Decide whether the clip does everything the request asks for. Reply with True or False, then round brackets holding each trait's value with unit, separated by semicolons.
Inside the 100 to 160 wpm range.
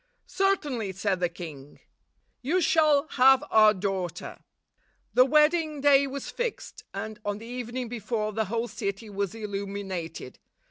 True (135 wpm)